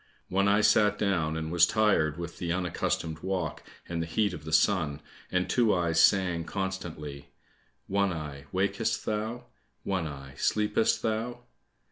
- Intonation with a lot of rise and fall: No, average, 4.1 semitones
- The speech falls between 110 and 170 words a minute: Yes, average, 150 wpm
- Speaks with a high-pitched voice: No, very low, 90 Hz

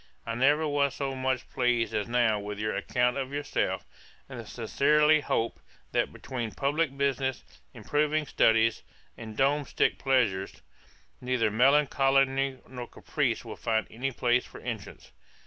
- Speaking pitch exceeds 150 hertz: No, low, 130 Hz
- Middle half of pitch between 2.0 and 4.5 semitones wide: Yes, average, 3.2 semitones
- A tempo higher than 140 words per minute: No, slow, 135 wpm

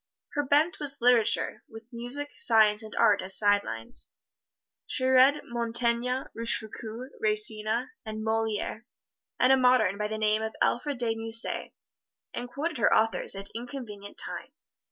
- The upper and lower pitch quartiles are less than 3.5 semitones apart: Yes, average, 2.9 semitones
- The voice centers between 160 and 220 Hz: No, high, 230 Hz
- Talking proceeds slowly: No, average, 145 wpm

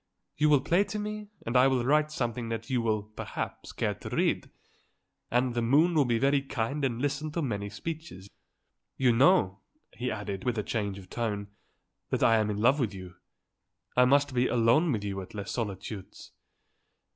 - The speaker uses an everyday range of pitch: Yes, average, 5.0 semitones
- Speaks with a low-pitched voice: Yes, low, 120 Hz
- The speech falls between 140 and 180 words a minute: No, average, 190 wpm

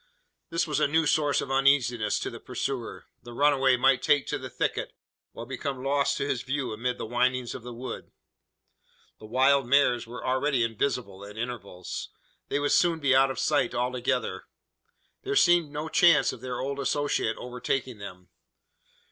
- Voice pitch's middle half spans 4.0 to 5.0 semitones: No, average, 2.9 semitones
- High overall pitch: No, low, 130 Hz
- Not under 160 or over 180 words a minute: Yes, average, 175 wpm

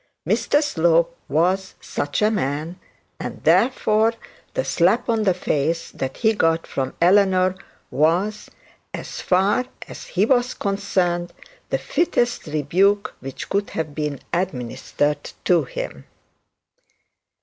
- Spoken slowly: Yes, slow, 120 wpm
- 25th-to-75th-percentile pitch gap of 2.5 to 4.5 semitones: No, average, 5.0 semitones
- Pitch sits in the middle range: Yes, medium, 180 Hz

